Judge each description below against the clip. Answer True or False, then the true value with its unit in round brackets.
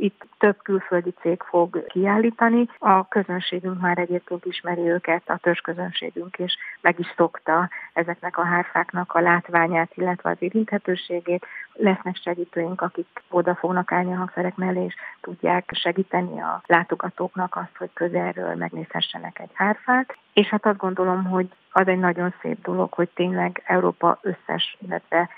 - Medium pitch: True (180 Hz)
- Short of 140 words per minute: False (145 wpm)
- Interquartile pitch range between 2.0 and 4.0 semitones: False (1.5 semitones)